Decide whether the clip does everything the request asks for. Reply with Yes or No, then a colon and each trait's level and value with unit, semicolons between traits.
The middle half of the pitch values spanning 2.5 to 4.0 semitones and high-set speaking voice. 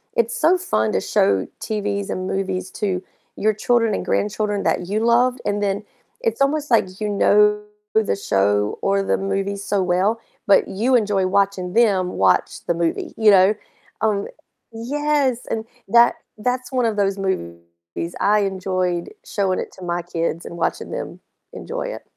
Yes: average, 3.4 semitones; high, 200 Hz